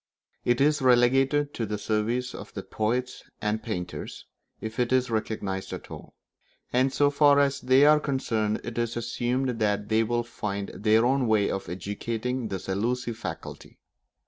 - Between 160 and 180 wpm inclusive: Yes, average, 165 wpm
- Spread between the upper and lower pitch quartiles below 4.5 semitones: Yes, average, 3.2 semitones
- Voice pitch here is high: No, low, 120 Hz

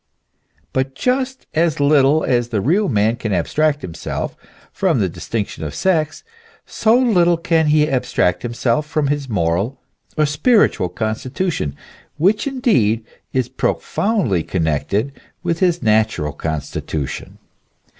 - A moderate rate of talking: No, slow, 125 wpm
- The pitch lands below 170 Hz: Yes, low, 135 Hz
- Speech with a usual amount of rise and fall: No, wide, 7.9 semitones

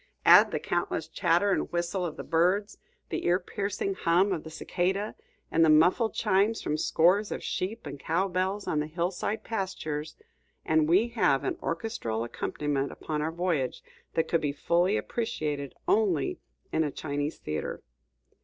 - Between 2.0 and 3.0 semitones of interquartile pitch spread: No, average, 4.1 semitones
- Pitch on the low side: No, medium, 170 Hz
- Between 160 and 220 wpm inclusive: Yes, average, 165 wpm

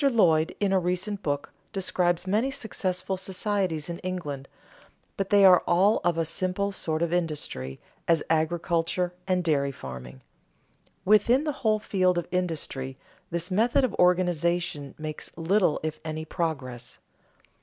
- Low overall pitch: No, medium, 175 Hz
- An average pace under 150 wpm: Yes, average, 140 wpm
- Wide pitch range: No, average, 3.5 semitones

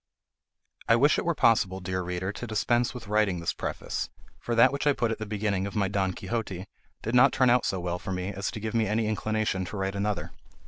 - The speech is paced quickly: Yes, fast, 235 wpm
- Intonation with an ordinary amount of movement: Yes, average, 3.3 semitones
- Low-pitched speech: Yes, low, 105 Hz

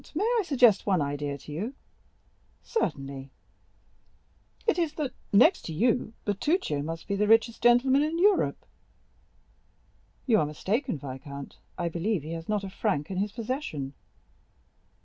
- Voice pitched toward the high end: Yes, high, 205 Hz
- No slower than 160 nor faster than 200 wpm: No, average, 150 wpm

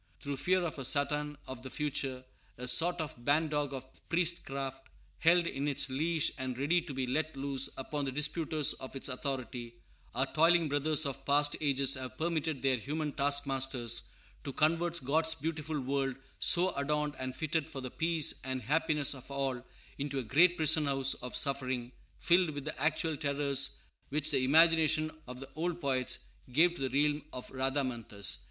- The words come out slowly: No, average, 175 wpm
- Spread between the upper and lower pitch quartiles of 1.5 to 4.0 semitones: Yes, average, 2.9 semitones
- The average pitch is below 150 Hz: Yes, medium, 140 Hz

